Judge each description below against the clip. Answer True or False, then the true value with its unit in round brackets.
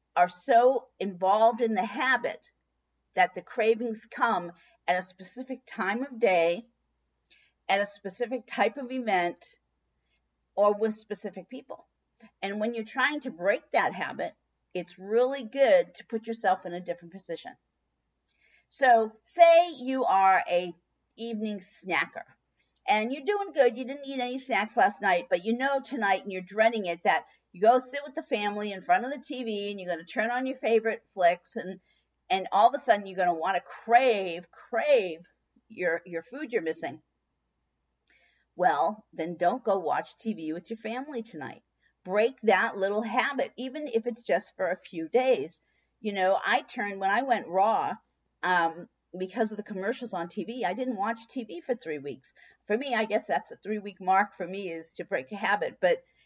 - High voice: True (220 Hz)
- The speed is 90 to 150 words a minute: False (180 wpm)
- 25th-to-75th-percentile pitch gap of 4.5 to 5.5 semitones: True (5.2 semitones)